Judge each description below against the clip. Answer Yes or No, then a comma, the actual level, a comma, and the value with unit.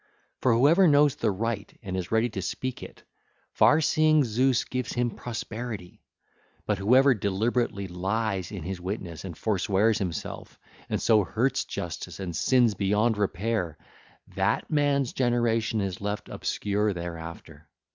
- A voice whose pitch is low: Yes, low, 110 Hz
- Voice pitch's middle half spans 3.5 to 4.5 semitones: Yes, average, 4.2 semitones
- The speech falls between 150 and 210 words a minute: No, average, 140 wpm